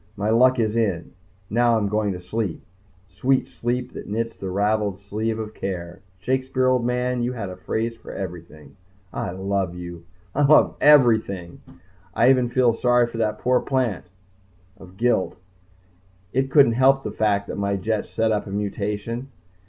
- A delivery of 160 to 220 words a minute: Yes, average, 170 wpm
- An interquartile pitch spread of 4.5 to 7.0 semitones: No, average, 3.8 semitones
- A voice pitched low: Yes, low, 110 Hz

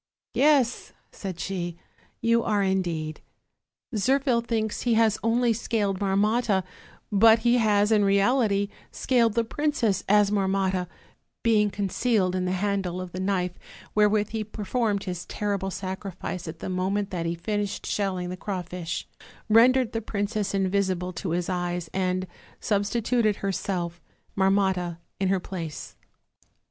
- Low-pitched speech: No, high, 200 Hz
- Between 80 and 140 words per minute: Yes, slow, 135 wpm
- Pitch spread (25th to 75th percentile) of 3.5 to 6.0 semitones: No, average, 3.0 semitones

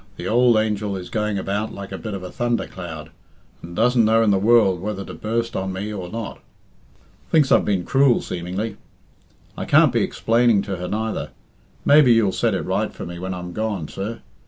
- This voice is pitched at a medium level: No, low, 105 Hz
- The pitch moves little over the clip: No, average, 3.3 semitones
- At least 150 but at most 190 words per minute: No, fast, 205 wpm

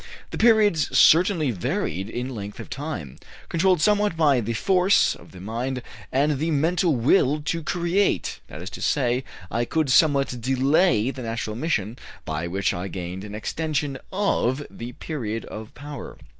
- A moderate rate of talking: Yes, average, 160 wpm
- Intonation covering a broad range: Yes, wide, 6.4 semitones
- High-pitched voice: No, low, 135 Hz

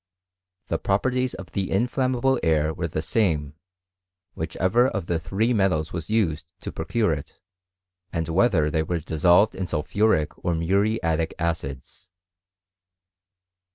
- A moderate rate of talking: No, slow, 130 wpm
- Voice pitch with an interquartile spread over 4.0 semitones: Yes, average, 5.2 semitones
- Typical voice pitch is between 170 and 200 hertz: No, very low, 90 Hz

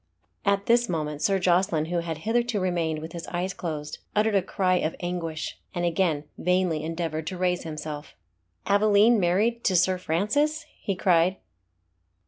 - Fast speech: No, average, 155 wpm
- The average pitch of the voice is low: No, medium, 180 Hz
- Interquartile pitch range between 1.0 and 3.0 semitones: No, average, 3.5 semitones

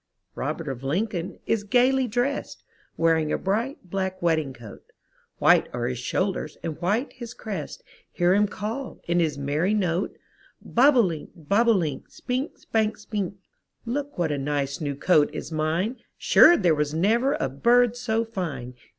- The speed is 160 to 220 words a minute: Yes, average, 165 wpm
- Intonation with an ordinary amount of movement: No, wide, 6.8 semitones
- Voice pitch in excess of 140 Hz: Yes, medium, 185 Hz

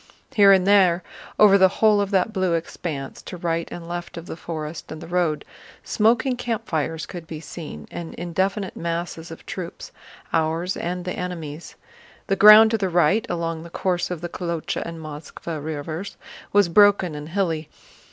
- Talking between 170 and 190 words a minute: No, average, 160 wpm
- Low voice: No, medium, 175 Hz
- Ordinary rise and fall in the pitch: Yes, average, 3.1 semitones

